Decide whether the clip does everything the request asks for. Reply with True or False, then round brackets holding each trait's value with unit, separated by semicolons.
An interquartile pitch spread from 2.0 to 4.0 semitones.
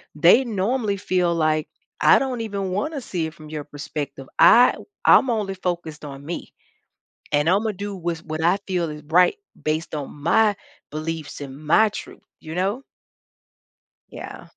False (4.7 semitones)